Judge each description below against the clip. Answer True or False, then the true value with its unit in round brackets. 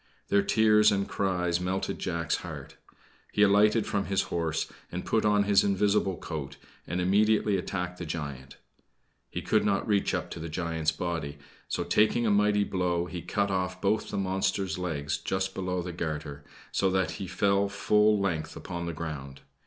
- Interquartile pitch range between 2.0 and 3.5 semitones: True (3.0 semitones)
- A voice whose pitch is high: False (95 Hz)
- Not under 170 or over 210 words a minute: True (175 wpm)